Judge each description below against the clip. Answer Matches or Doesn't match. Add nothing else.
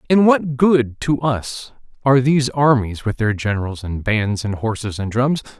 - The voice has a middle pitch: Doesn't match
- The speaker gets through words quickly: Doesn't match